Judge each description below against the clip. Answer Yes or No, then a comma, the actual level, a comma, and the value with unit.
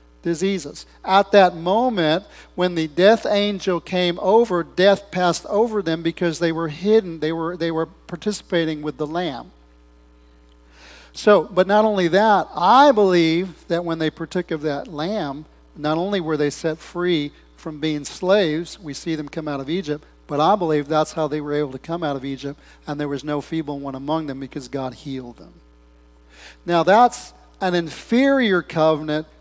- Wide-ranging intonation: No, average, 3.7 semitones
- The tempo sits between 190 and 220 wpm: No, average, 175 wpm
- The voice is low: No, medium, 160 Hz